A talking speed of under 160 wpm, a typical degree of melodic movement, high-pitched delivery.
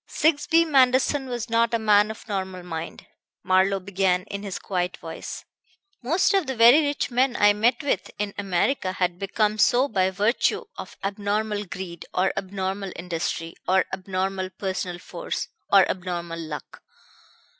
Yes: average, 150 wpm; average, 3.9 semitones; high, 200 Hz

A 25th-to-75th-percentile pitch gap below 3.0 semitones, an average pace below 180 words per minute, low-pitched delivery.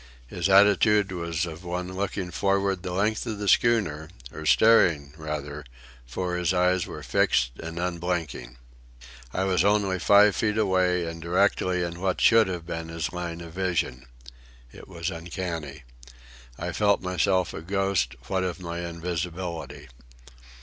Yes: narrow, 2.6 semitones; average, 150 wpm; very low, 90 Hz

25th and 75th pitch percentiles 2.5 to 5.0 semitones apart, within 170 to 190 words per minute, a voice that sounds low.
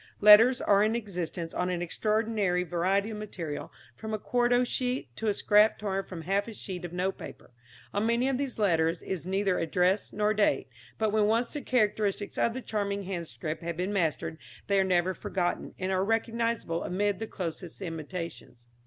No: average, 3.5 semitones; average, 185 wpm; high, 200 Hz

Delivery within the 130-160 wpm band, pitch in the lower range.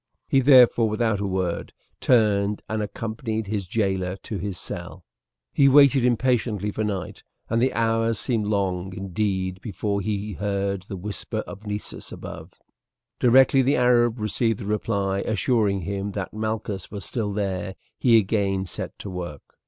Yes: average, 150 wpm; low, 105 Hz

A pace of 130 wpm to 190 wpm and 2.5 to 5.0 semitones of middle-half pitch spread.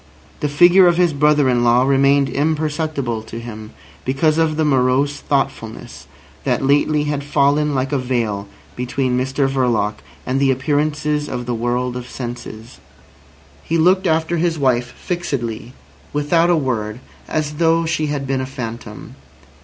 Yes: average, 155 wpm; average, 3.5 semitones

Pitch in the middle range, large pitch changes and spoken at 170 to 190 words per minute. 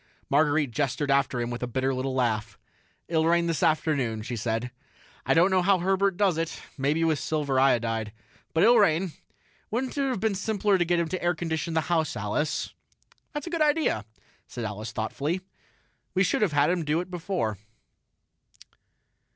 Yes: medium, 160 Hz; wide, 6.0 semitones; average, 180 wpm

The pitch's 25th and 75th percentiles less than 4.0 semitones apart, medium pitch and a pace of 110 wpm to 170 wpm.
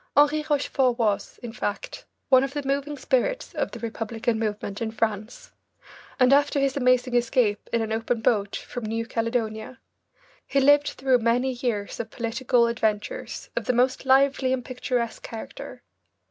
No: average, 2.9 semitones; high, 245 Hz; average, 160 wpm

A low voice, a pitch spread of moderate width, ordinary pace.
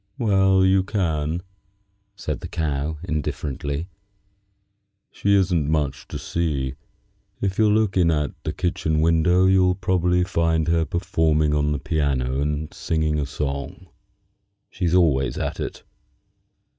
No: very low, 80 Hz; average, 3.6 semitones; slow, 130 wpm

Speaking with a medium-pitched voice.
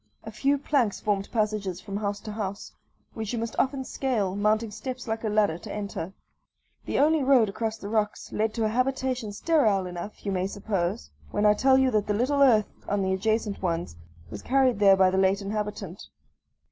No: high, 210 Hz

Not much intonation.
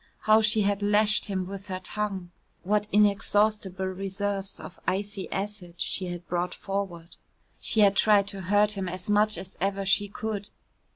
Yes: narrow, 1.7 semitones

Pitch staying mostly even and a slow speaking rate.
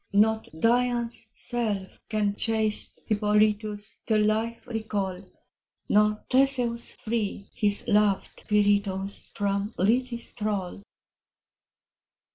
Yes: narrow, 2.1 semitones; slow, 85 wpm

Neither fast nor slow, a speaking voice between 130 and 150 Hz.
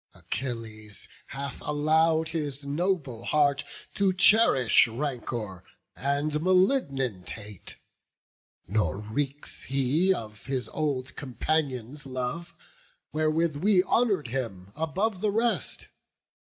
No: slow, 100 wpm; medium, 140 Hz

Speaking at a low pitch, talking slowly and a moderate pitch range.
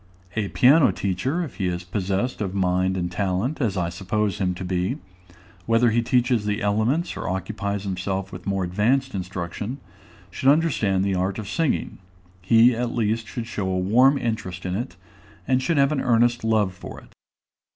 No: low, 105 Hz; average, 180 wpm; average, 4.6 semitones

